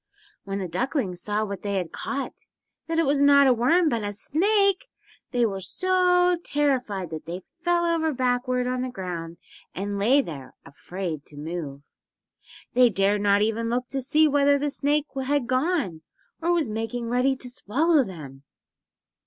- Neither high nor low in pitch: No, high, 245 Hz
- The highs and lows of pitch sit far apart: Yes, wide, 6.8 semitones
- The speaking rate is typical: Yes, average, 160 wpm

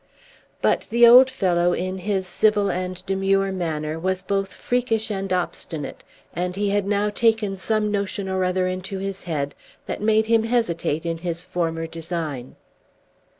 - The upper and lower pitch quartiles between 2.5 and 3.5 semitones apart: Yes, average, 3.0 semitones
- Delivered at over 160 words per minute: No, average, 155 wpm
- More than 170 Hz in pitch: Yes, high, 190 Hz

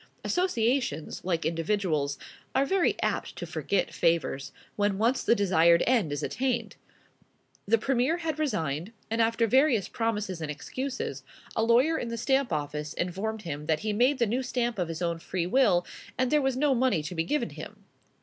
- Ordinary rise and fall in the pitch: No, wide, 7.3 semitones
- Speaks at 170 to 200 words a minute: Yes, average, 180 wpm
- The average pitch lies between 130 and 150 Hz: No, high, 220 Hz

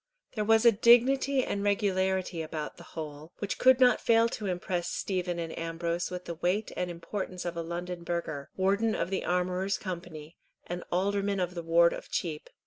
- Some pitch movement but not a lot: Yes, average, 3.0 semitones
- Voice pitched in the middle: Yes, medium, 180 Hz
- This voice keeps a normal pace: Yes, average, 185 wpm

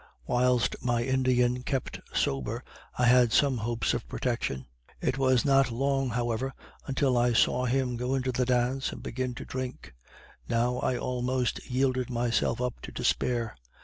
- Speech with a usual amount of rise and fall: No, narrow, 1.4 semitones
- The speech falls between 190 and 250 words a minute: No, average, 155 wpm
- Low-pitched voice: Yes, low, 125 Hz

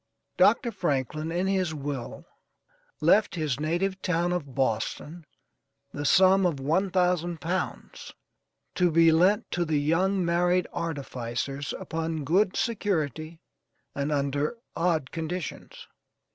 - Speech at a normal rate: No, slow, 115 wpm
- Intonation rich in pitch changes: No, average, 3.7 semitones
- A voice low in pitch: No, medium, 165 Hz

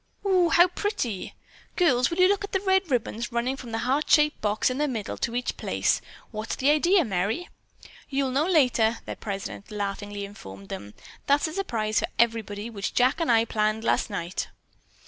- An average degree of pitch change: No, wide, 6.3 semitones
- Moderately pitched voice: No, high, 240 Hz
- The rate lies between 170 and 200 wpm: Yes, average, 190 wpm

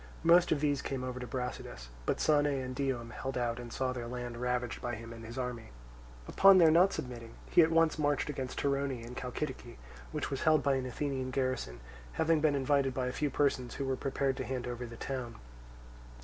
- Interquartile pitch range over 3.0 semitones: No, narrow, 2.6 semitones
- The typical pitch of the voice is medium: No, low, 130 Hz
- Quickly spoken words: Yes, fast, 210 wpm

